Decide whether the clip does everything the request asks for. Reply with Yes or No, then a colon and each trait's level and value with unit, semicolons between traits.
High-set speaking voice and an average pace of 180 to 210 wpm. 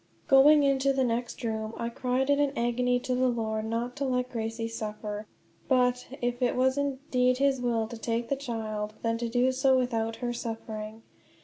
Yes: high, 245 Hz; average, 190 wpm